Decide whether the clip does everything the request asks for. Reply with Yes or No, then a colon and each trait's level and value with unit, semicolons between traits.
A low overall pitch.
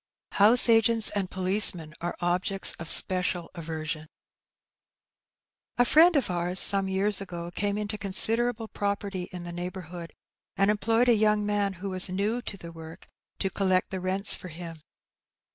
No: high, 190 Hz